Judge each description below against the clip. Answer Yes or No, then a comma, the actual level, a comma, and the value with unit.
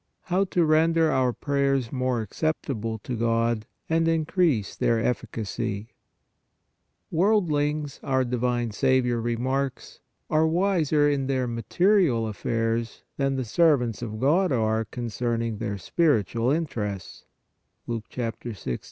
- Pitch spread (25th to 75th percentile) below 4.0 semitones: No, average, 5.1 semitones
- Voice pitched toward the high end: No, low, 125 Hz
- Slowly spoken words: Yes, slow, 115 wpm